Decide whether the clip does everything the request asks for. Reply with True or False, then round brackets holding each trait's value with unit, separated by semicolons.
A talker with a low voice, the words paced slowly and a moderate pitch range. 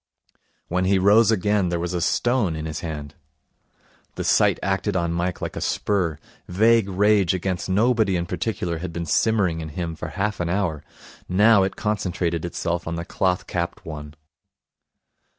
False (90 Hz; 170 wpm; 3.3 semitones)